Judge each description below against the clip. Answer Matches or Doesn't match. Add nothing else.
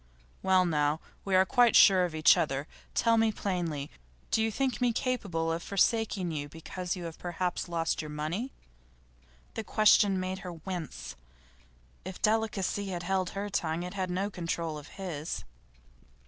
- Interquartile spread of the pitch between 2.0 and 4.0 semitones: Matches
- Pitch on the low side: Doesn't match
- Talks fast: Doesn't match